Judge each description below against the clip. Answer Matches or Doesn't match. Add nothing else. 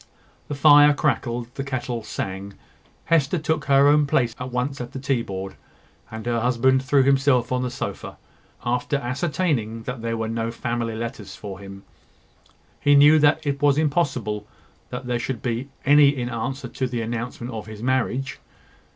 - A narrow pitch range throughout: Doesn't match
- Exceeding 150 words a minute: Matches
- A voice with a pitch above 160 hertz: Doesn't match